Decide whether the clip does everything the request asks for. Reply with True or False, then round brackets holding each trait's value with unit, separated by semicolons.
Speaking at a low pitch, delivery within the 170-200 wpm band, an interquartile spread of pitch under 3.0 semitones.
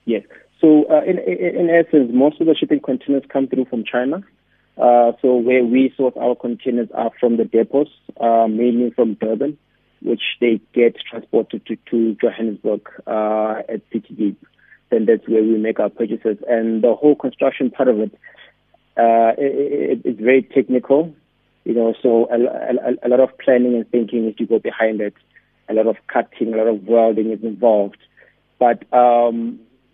True (120 Hz; 180 wpm; 2.6 semitones)